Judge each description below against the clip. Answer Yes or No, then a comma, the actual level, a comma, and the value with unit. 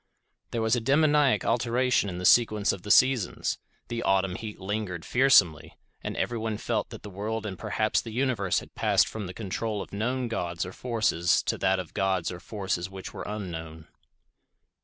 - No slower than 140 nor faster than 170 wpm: No, average, 180 wpm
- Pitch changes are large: No, average, 3.9 semitones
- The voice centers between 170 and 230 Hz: No, low, 105 Hz